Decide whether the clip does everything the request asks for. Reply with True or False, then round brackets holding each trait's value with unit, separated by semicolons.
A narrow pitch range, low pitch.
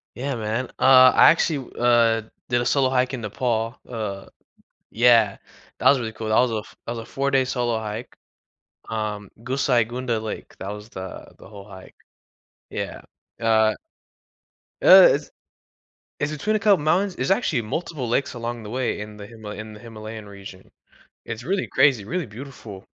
False (3.3 semitones; 115 Hz)